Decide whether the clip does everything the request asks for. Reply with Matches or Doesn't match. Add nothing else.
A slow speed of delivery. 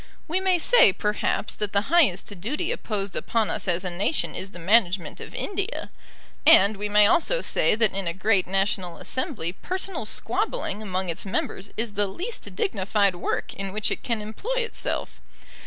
Doesn't match